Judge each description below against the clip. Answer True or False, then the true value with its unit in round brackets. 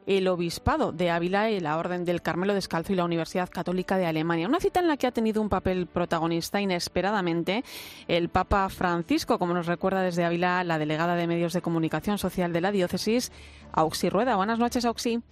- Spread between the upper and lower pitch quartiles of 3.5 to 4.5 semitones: False (2.9 semitones)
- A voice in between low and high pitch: True (180 Hz)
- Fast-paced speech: True (195 wpm)